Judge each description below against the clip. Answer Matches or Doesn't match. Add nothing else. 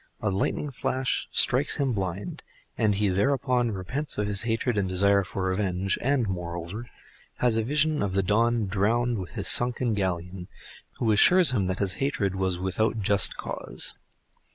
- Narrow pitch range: Doesn't match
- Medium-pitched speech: Doesn't match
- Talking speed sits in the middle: Matches